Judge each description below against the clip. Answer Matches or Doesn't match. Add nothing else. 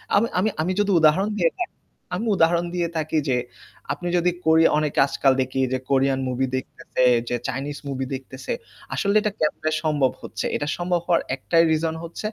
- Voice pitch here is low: Doesn't match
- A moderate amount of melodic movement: Matches